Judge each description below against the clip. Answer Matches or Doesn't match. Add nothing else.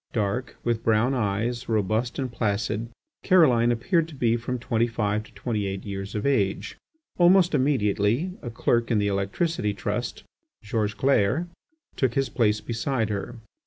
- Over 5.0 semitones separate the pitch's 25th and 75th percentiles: Doesn't match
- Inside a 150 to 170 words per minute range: Matches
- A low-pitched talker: Matches